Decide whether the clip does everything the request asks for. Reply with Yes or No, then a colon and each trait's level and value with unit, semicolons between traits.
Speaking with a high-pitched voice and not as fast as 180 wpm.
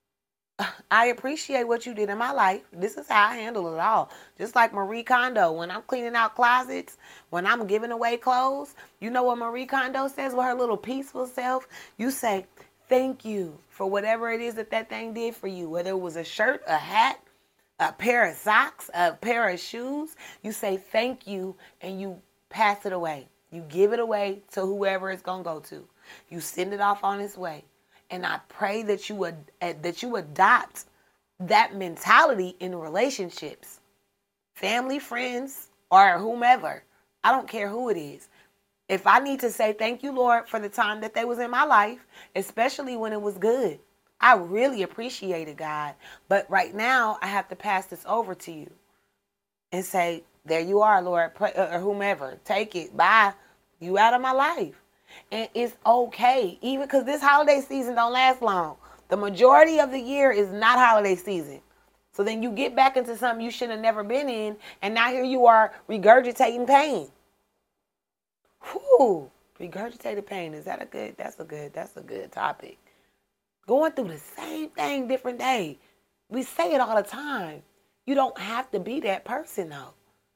No: high, 220 Hz; average, 185 wpm